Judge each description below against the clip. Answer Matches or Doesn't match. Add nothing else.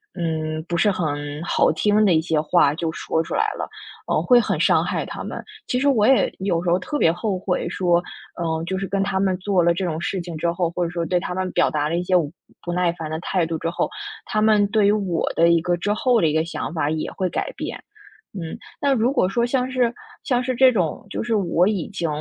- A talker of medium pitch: Matches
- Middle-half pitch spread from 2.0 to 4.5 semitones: Matches